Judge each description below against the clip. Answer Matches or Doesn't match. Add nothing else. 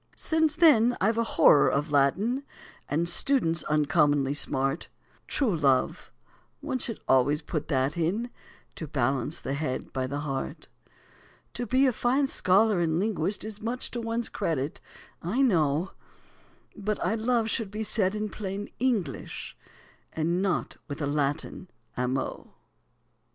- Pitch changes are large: Matches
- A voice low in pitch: Doesn't match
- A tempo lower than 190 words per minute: Matches